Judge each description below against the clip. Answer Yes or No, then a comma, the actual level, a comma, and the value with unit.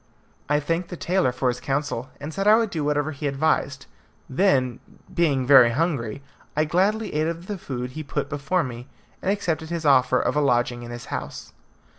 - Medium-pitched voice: Yes, medium, 145 Hz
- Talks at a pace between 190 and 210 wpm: Yes, average, 195 wpm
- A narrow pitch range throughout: No, average, 4.6 semitones